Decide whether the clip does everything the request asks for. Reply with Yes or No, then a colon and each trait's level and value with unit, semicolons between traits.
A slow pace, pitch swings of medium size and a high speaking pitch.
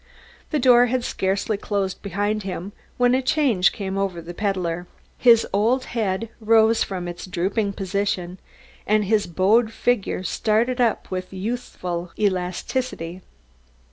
Yes: slow, 130 wpm; average, 3.7 semitones; high, 200 Hz